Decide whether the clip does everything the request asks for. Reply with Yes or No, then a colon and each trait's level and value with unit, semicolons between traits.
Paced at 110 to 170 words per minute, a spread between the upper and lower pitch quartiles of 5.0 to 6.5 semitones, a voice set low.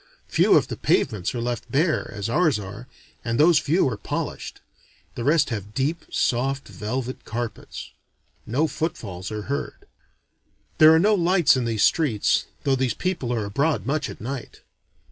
Yes: average, 165 wpm; wide, 5.5 semitones; low, 130 Hz